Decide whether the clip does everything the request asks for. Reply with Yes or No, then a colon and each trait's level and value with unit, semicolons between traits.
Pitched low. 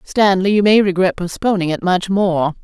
No: high, 190 Hz